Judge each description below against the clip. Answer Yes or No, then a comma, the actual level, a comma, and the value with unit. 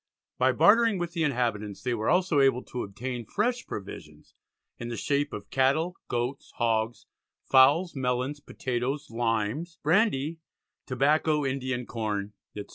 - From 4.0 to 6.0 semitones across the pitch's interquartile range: Yes, average, 4.4 semitones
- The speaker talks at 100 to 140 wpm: Yes, slow, 135 wpm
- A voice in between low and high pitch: No, low, 130 Hz